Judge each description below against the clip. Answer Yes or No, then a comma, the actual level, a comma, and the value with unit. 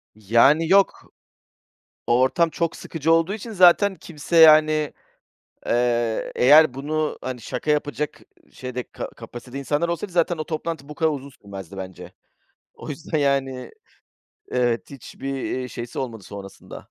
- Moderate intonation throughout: Yes, average, 4.7 semitones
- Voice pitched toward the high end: No, medium, 145 Hz